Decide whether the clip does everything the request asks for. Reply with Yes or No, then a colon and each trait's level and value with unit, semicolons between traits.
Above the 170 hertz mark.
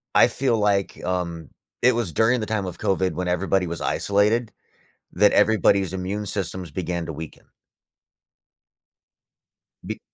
No: very low, 95 Hz